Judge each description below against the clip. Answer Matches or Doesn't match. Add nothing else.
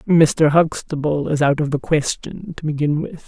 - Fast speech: Doesn't match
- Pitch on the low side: Doesn't match